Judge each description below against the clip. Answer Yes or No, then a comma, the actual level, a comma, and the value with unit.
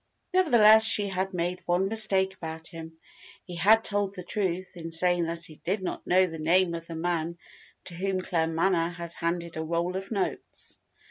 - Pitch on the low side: No, medium, 180 Hz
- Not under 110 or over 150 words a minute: No, average, 185 wpm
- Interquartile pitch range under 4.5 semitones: Yes, narrow, 2.4 semitones